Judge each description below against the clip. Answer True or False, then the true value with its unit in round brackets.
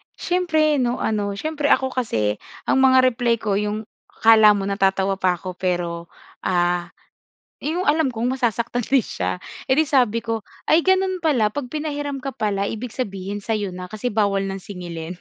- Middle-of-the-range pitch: False (220 Hz)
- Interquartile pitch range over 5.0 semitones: True (5.5 semitones)